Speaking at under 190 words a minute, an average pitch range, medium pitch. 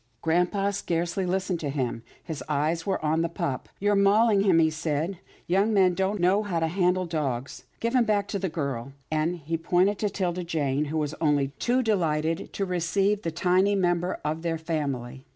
No: fast, 205 wpm; average, 4.0 semitones; medium, 170 Hz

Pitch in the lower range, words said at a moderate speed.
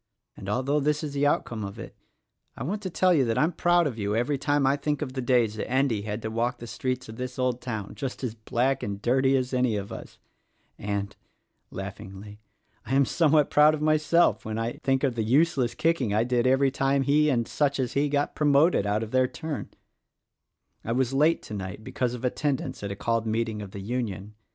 No: low, 125 Hz; fast, 220 wpm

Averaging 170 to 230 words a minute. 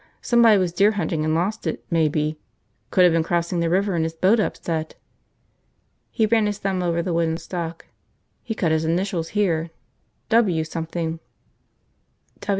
No: average, 155 wpm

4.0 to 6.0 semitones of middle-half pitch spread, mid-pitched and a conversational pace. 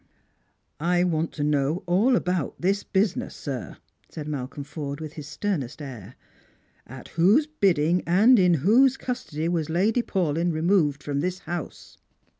Yes: average, 4.5 semitones; medium, 170 Hz; average, 150 wpm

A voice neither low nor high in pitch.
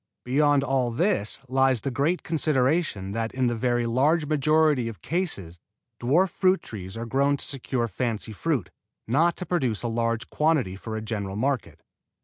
No: low, 130 Hz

